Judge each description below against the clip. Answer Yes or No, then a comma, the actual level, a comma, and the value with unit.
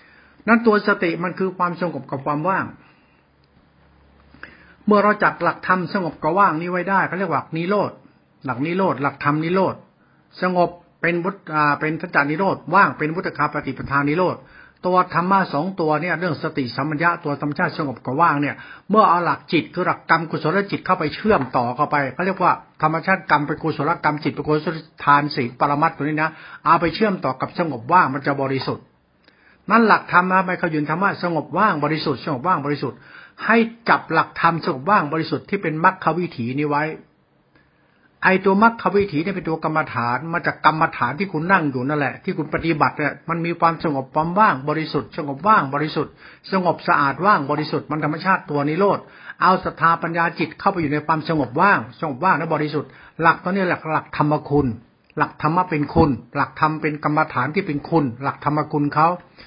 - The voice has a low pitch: No, medium, 160 Hz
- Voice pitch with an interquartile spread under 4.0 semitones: Yes, average, 3.6 semitones